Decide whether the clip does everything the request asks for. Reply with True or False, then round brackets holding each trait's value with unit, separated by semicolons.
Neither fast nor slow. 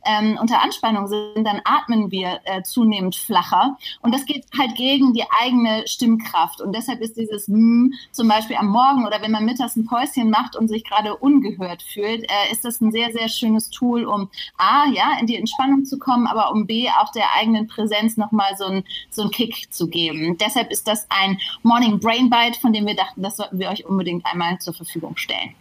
False (210 wpm)